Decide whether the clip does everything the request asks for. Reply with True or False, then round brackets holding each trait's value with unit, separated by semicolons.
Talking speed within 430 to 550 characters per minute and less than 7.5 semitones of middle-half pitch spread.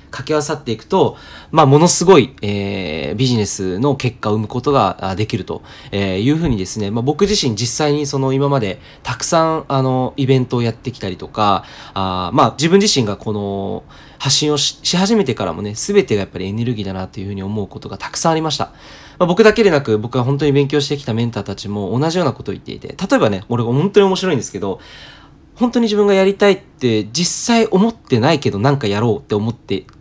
True (450 characters per minute; 6.8 semitones)